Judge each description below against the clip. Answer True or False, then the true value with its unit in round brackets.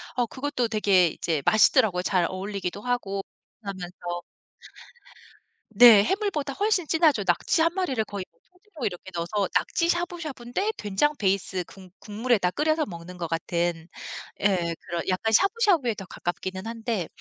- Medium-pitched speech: False (210 Hz)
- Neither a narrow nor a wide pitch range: False (8.2 semitones)